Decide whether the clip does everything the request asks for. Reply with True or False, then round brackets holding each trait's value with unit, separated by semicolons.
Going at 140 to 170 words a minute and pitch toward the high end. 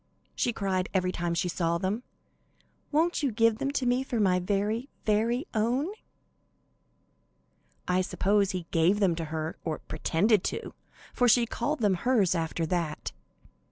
True (155 wpm; 200 Hz)